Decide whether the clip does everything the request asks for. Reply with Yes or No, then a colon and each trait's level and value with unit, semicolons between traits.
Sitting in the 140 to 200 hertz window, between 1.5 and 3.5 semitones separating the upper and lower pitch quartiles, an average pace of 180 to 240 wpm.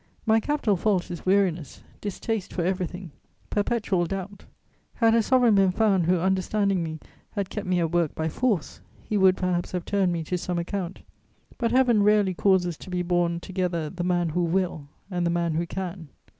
Yes: medium, 185 Hz; average, 2.7 semitones; average, 185 wpm